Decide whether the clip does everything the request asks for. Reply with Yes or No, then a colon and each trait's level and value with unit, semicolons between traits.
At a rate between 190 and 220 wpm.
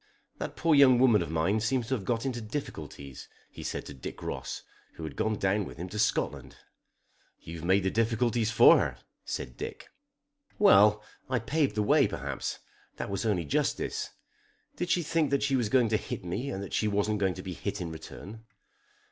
Yes: average, 200 wpm